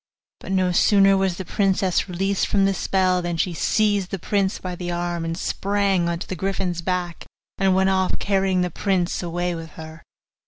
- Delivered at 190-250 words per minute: Yes, average, 195 wpm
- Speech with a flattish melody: Yes, narrow, 1.9 semitones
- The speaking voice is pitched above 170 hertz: Yes, medium, 185 Hz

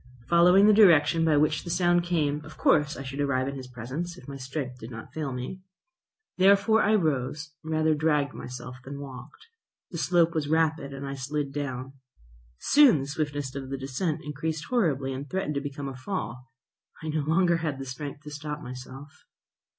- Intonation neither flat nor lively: Yes, average, 3.2 semitones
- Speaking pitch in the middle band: Yes, medium, 145 Hz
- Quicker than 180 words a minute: Yes, average, 190 wpm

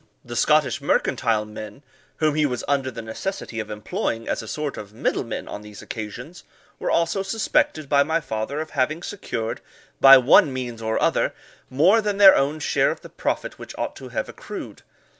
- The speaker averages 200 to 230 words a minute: No, average, 190 wpm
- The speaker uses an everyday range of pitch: No, wide, 5.7 semitones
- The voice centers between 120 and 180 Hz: Yes, low, 135 Hz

